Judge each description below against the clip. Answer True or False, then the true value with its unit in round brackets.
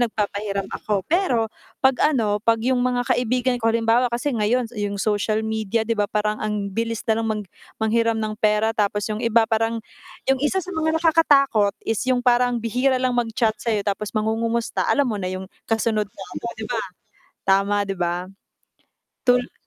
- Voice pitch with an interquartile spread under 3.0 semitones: True (2.6 semitones)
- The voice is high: True (225 Hz)